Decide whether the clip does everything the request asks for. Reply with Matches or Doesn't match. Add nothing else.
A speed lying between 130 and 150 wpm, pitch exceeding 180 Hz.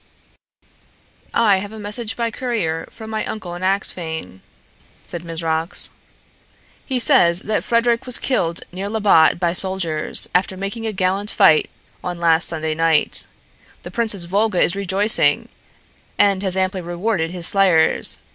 Matches